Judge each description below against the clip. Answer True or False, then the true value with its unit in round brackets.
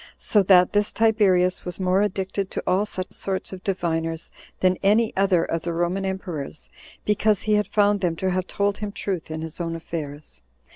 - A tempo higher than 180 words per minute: True (190 wpm)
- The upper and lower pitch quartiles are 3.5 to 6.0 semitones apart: False (3.0 semitones)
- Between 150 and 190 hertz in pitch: True (185 Hz)